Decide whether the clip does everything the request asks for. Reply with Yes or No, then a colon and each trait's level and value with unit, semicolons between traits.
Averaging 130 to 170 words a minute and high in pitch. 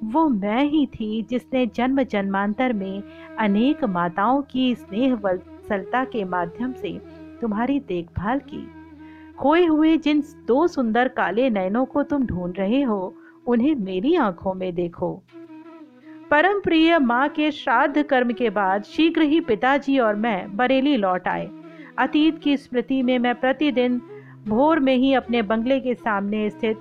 Yes: average, 150 wpm; very high, 255 Hz